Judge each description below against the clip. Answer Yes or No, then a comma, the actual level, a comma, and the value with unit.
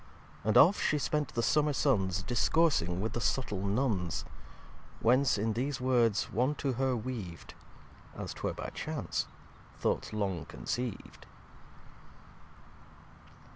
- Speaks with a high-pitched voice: No, low, 120 Hz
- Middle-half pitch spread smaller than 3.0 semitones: No, average, 5.0 semitones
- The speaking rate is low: Yes, slow, 120 wpm